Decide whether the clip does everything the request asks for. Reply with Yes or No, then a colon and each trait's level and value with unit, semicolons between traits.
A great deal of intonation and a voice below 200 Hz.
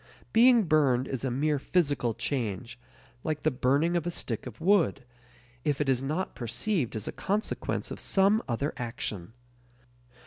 Yes: wide, 5.8 semitones; medium, 140 Hz